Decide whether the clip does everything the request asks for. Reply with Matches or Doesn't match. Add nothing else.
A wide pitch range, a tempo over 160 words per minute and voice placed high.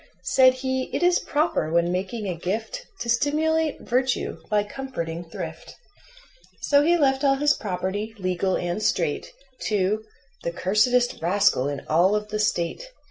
Doesn't match